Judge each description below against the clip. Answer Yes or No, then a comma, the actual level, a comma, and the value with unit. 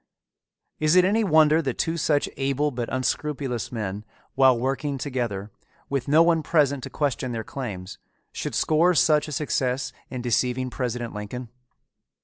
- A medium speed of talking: Yes, average, 150 wpm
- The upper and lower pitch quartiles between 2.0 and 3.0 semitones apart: No, average, 3.7 semitones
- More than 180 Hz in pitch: No, low, 135 Hz